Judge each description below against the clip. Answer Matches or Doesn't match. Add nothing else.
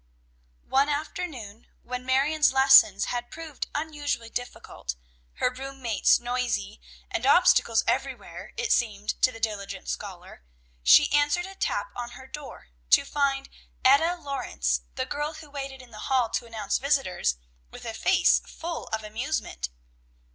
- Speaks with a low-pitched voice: Doesn't match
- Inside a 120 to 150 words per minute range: Matches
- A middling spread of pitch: Matches